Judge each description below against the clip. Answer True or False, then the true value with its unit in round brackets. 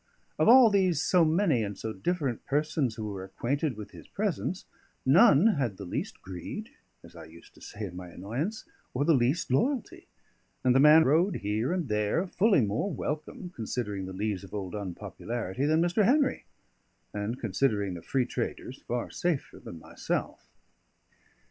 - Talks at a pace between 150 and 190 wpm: True (165 wpm)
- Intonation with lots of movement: True (8.7 semitones)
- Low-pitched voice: True (130 Hz)